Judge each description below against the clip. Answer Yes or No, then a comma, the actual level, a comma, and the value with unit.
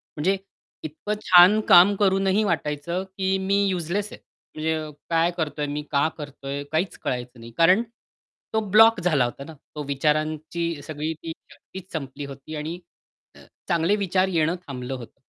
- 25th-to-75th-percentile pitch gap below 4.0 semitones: No, average, 4.4 semitones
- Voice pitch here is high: No, medium, 160 Hz